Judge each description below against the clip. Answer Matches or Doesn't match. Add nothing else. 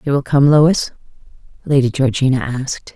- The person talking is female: Matches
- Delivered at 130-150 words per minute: Matches